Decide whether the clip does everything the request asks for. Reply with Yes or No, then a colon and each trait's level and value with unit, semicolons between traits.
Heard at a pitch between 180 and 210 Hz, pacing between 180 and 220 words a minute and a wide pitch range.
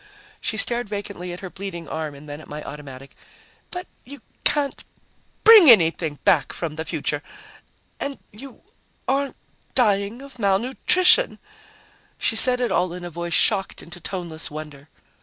No: high, 190 Hz; average, 150 wpm; wide, 7.5 semitones